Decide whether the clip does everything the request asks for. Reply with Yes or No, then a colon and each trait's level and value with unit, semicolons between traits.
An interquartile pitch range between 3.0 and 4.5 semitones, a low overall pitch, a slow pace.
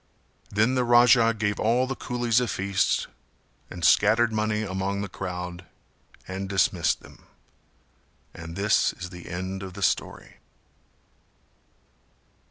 Yes: average, 3.7 semitones; low, 100 Hz; slow, 125 wpm